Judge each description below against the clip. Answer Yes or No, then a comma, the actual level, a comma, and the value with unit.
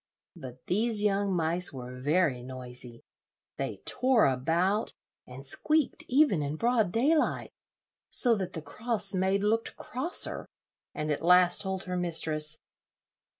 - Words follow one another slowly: Yes, slow, 130 wpm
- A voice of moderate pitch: Yes, medium, 180 Hz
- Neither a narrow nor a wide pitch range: No, wide, 6.3 semitones